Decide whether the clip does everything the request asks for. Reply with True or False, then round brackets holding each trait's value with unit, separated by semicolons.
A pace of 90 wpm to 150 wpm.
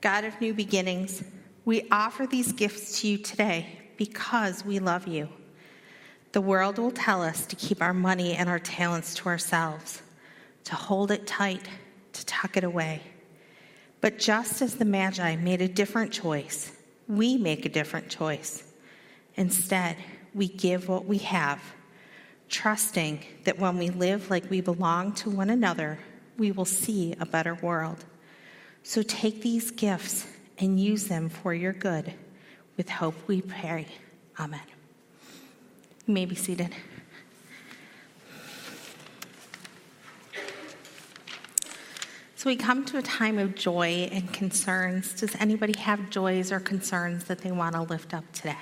True (145 wpm)